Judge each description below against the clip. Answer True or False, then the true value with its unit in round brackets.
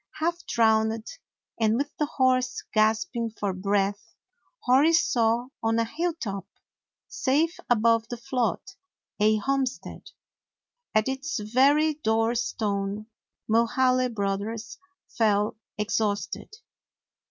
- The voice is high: True (230 Hz)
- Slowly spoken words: True (100 wpm)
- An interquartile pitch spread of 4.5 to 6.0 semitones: False (3.5 semitones)